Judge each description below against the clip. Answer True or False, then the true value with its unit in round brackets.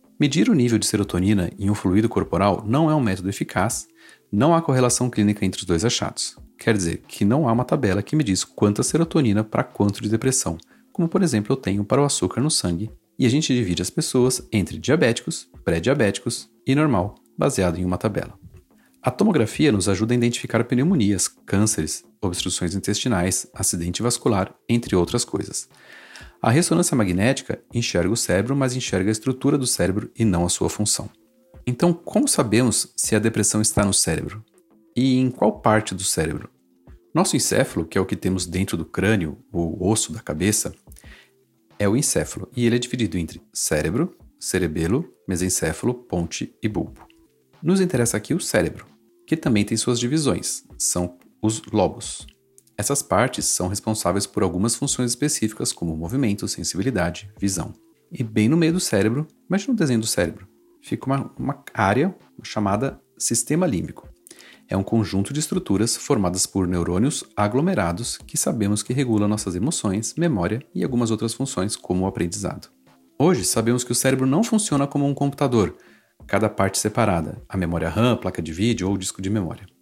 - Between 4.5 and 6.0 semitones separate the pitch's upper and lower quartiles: True (5.0 semitones)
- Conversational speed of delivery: True (170 wpm)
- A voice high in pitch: False (110 Hz)